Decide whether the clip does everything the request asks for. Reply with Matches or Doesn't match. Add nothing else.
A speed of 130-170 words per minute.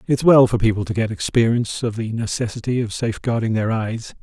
Doesn't match